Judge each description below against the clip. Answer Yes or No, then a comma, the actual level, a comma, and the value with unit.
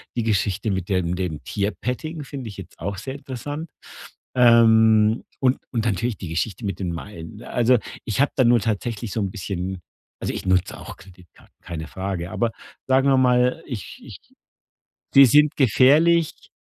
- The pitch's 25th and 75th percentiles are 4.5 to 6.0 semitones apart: Yes, average, 5.2 semitones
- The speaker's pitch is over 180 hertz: No, low, 110 Hz